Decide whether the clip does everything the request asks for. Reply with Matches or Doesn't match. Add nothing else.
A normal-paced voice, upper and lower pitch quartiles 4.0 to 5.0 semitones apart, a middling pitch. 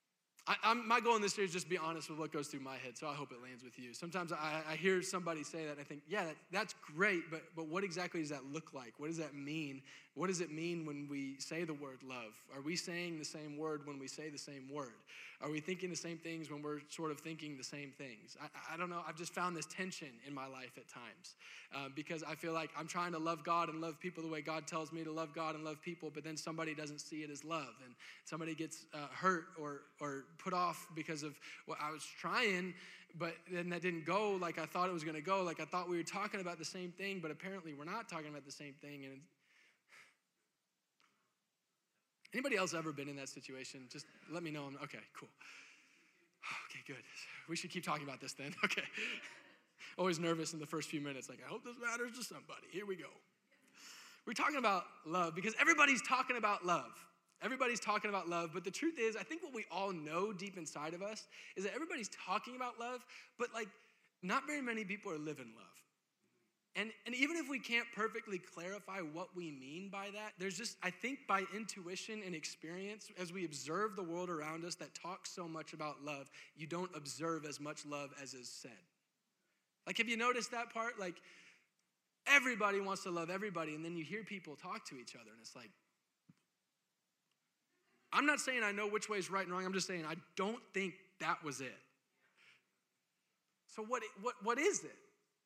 Doesn't match